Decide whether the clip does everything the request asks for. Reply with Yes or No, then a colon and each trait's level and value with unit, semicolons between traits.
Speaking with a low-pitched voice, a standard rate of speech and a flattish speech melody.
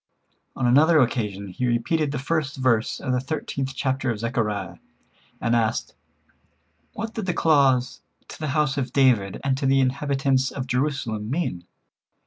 No: low, 130 Hz; average, 155 wpm; average, 3.3 semitones